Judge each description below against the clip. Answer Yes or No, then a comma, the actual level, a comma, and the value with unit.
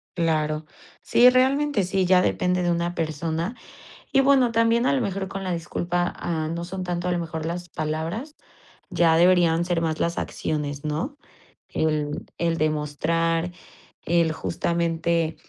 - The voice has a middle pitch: Yes, medium, 170 Hz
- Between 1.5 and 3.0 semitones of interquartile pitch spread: Yes, narrow, 2.4 semitones